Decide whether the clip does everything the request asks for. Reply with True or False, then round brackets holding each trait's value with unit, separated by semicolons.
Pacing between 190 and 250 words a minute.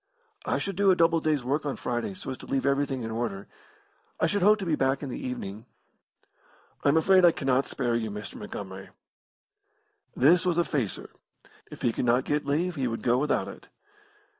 True (205 wpm)